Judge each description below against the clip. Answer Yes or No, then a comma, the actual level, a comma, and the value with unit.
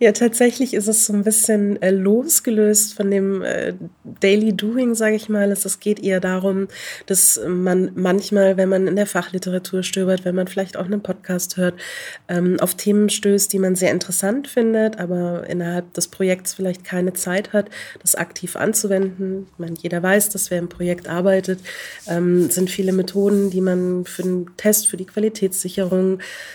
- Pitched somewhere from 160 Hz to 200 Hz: Yes, high, 190 Hz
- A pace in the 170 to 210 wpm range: Yes, average, 180 wpm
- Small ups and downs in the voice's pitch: Yes, narrow, 2.2 semitones